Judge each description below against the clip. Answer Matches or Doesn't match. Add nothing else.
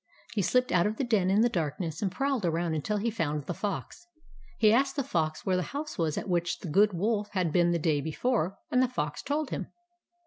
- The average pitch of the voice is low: Doesn't match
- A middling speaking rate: Doesn't match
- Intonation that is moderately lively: Doesn't match